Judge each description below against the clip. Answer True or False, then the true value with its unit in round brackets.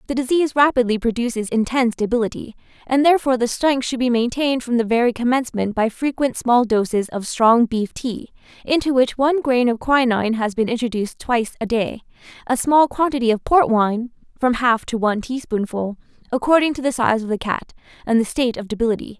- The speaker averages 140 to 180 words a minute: False (190 wpm)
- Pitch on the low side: False (240 Hz)